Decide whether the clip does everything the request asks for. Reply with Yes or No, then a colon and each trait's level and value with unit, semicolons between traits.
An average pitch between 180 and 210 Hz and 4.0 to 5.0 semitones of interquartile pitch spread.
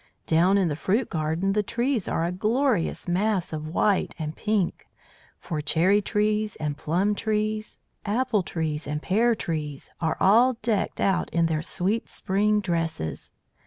Yes: high, 190 Hz; average, 4.7 semitones